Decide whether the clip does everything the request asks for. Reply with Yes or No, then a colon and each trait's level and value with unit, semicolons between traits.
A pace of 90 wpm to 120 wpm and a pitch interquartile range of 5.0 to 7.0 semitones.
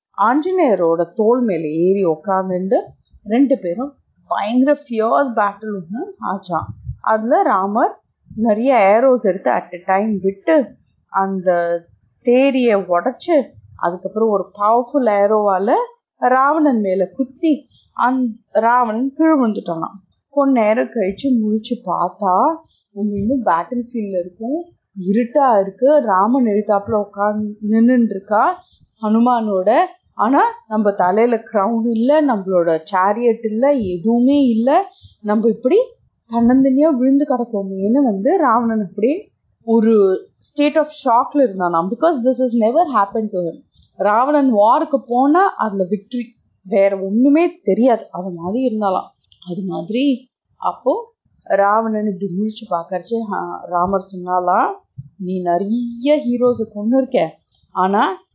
Yes: average, 110 wpm; wide, 5.4 semitones